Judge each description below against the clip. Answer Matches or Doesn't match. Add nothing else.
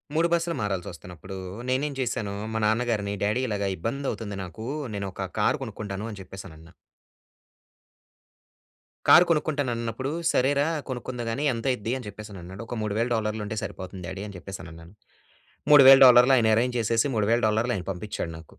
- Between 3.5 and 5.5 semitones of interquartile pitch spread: Matches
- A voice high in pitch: Doesn't match